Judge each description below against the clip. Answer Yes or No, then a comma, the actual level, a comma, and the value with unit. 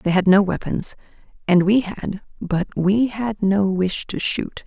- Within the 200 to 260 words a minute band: No, average, 180 wpm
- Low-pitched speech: No, high, 200 Hz